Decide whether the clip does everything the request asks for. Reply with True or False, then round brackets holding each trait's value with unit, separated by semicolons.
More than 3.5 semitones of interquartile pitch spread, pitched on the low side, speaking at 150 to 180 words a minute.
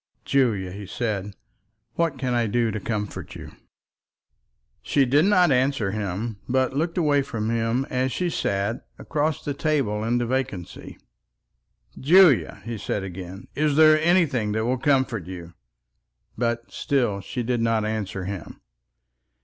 False (5.1 semitones; 120 Hz; 140 wpm)